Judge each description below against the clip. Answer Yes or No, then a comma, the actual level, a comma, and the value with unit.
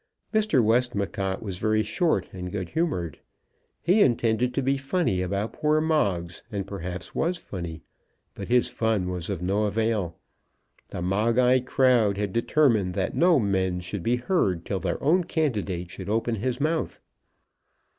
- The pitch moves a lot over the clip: Yes, wide, 5.7 semitones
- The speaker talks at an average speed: Yes, average, 155 wpm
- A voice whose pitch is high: No, low, 110 Hz